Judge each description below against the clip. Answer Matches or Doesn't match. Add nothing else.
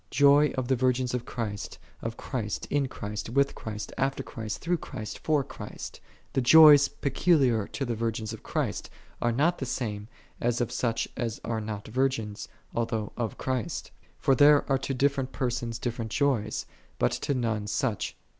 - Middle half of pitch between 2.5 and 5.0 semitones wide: Matches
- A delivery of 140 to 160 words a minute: Doesn't match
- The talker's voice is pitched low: Matches